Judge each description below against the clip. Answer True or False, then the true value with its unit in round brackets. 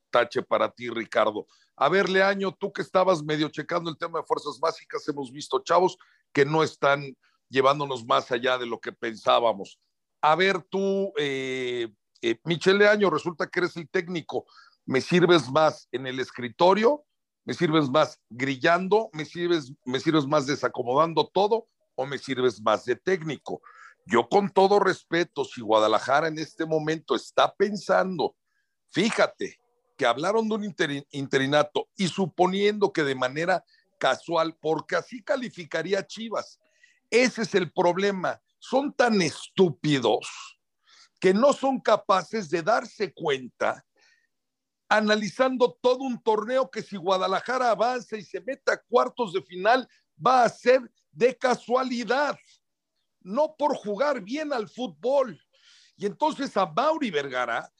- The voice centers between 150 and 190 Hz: True (185 Hz)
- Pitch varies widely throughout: True (7.0 semitones)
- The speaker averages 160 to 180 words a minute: False (145 wpm)